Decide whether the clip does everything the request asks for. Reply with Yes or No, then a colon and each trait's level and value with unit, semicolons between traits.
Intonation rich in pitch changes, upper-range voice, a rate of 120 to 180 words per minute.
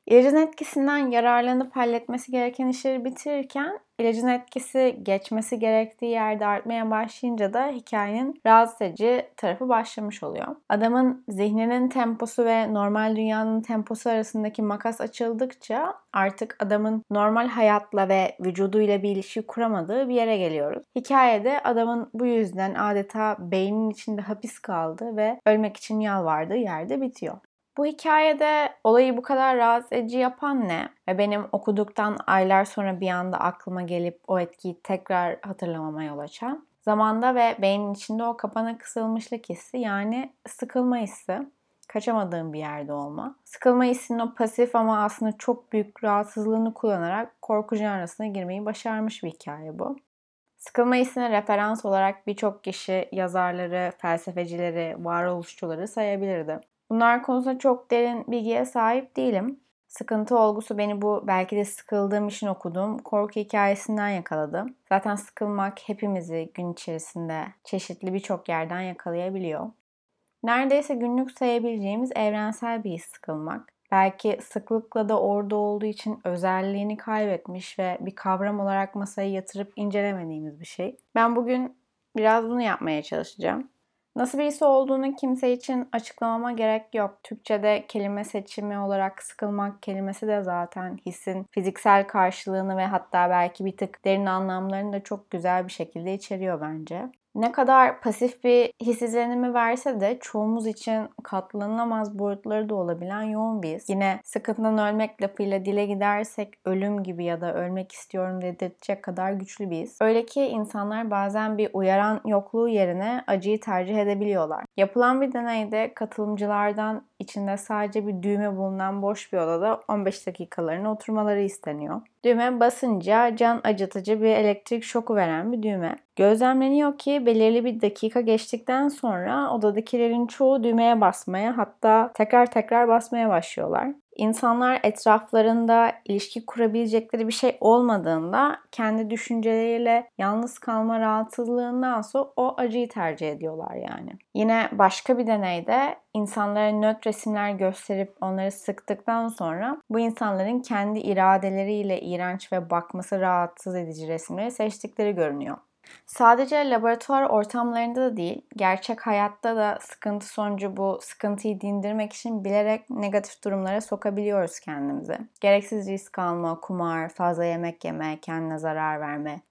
No: average, 3.3 semitones; high, 215 Hz; average, 130 wpm